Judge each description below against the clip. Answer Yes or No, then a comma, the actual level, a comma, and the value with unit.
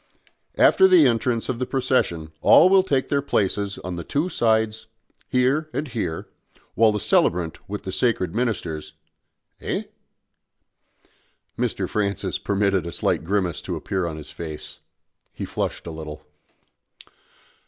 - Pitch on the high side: No, low, 105 Hz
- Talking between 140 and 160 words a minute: Yes, average, 145 wpm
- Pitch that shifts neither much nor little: No, wide, 6.7 semitones